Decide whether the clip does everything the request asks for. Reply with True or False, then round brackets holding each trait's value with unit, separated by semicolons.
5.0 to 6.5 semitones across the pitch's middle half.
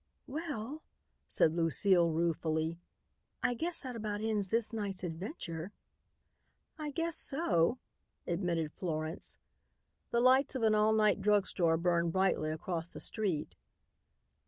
True (5.6 semitones)